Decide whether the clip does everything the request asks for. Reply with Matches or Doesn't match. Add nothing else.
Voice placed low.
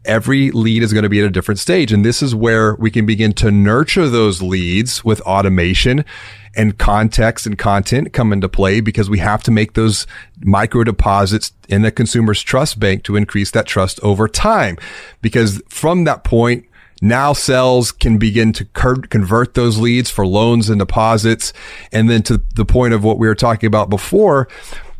Matches